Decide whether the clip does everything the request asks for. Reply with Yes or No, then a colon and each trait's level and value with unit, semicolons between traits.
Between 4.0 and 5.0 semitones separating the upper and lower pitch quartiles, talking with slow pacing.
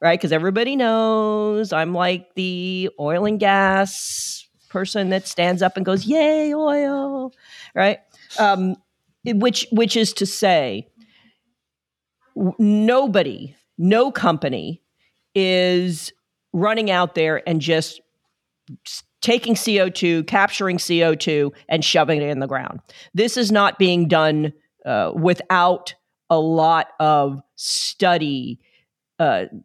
Yes: average, 4.7 semitones; slow, 120 wpm